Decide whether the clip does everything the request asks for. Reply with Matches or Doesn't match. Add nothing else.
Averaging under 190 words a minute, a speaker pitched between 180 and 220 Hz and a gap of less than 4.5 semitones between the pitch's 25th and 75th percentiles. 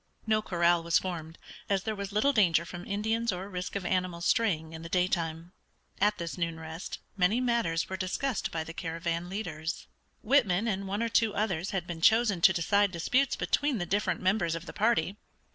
Doesn't match